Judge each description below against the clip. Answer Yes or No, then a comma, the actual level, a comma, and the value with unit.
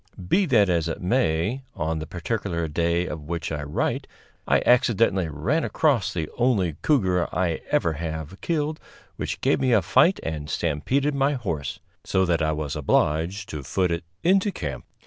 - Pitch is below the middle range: Yes, very low, 90 Hz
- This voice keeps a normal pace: Yes, average, 170 wpm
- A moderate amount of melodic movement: No, wide, 7.5 semitones